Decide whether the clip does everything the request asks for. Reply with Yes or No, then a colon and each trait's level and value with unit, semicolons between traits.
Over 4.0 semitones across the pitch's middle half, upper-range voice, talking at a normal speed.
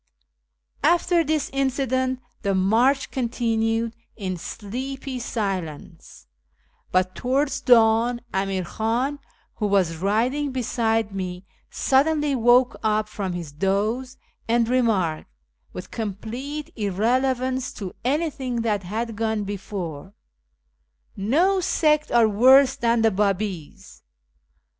No: average, 4.8 semitones; high, 225 Hz; slow, 105 wpm